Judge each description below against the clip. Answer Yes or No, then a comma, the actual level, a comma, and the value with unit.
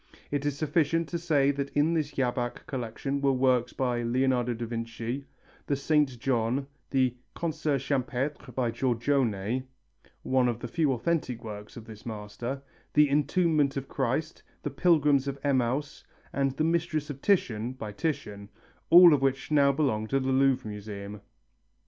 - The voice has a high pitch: No, low, 135 Hz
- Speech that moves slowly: No, average, 155 wpm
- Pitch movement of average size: Yes, average, 3.5 semitones